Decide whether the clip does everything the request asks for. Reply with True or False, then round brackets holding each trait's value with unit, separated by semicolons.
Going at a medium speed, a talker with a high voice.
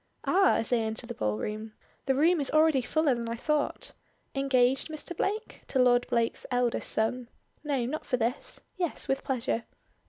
True (175 wpm; 255 Hz)